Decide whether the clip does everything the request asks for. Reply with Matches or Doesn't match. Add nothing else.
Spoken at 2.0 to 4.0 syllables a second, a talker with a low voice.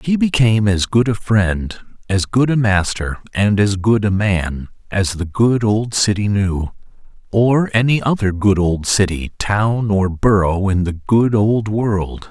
Matches